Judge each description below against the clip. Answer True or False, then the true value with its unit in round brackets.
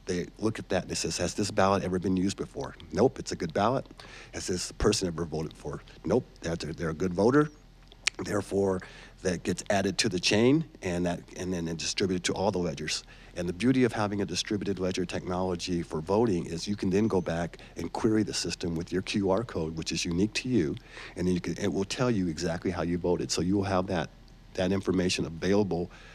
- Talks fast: True (220 wpm)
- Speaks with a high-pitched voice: False (95 Hz)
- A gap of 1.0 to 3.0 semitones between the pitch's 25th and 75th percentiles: True (2.6 semitones)